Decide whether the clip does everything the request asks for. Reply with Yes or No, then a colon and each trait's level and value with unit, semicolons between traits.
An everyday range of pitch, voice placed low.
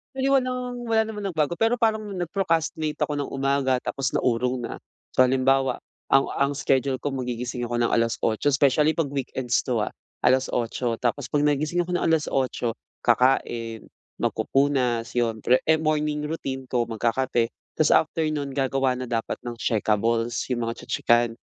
Yes: average, 4.0 semitones; low, 130 Hz